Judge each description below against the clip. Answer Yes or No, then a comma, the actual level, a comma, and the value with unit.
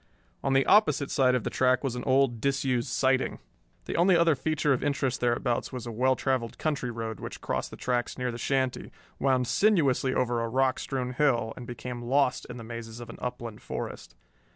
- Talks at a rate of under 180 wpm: No, average, 200 wpm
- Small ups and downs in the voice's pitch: Yes, narrow, 2.2 semitones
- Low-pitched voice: Yes, low, 125 Hz